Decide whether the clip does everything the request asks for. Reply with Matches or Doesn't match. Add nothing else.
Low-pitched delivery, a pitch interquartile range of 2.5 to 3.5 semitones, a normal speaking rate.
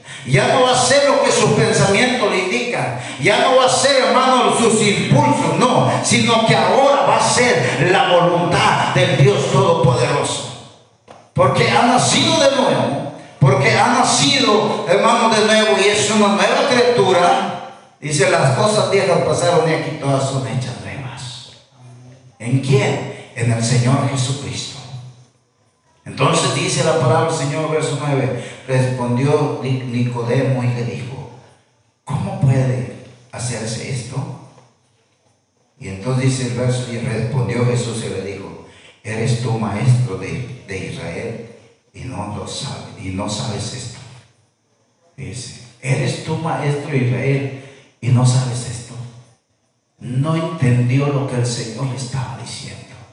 Matches